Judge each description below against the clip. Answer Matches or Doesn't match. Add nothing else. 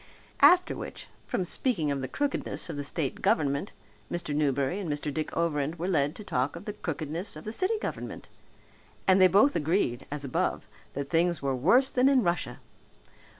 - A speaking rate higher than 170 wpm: Matches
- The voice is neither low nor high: Matches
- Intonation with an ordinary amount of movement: Doesn't match